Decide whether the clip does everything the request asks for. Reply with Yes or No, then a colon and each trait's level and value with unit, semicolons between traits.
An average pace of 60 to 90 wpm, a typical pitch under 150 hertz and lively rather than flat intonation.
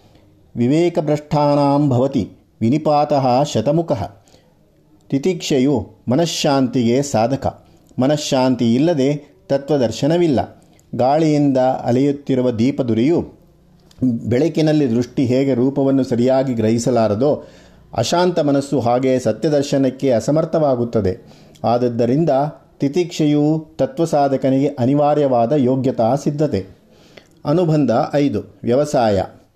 No: slow, 65 wpm; low, 135 Hz; average, 3.3 semitones